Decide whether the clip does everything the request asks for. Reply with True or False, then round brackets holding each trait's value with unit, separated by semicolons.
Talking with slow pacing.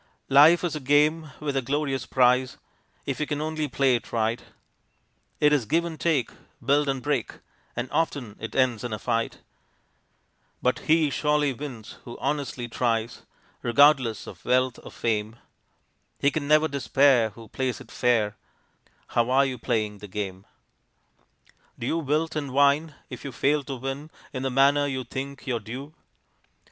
False (165 wpm)